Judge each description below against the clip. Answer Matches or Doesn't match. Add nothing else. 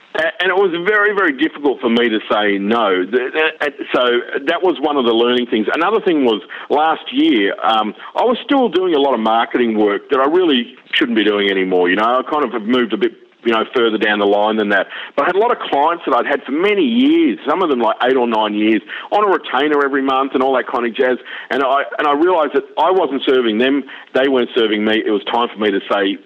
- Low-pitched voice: Matches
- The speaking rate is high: Matches